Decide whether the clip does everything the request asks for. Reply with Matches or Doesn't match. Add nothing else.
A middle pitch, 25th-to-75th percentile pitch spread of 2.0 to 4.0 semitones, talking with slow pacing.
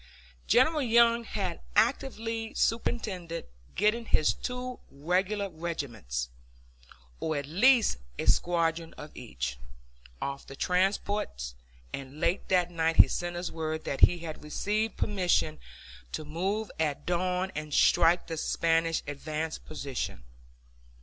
Doesn't match